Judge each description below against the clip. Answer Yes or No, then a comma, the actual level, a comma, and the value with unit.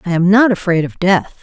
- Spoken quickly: Yes, fast, 255 wpm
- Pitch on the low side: No, medium, 185 Hz